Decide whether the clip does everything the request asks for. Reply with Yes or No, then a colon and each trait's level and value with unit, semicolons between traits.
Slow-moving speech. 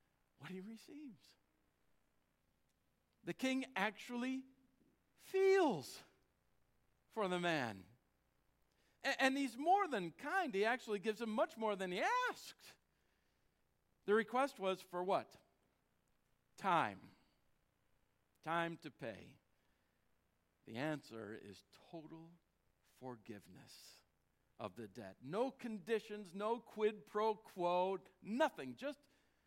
Yes: slow, 100 wpm